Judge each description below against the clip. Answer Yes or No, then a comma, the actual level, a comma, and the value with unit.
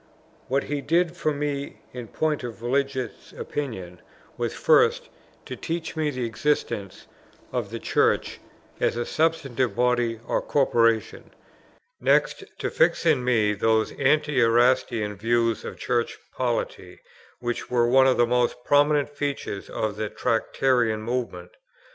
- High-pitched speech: No, low, 125 Hz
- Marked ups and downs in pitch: No, average, 4.0 semitones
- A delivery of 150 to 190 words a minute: No, slow, 135 wpm